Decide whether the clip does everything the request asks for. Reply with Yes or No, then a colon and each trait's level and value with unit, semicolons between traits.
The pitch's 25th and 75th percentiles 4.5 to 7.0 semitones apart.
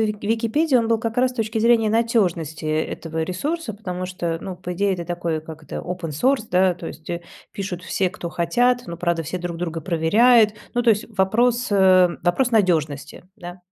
Yes: average, 4.9 semitones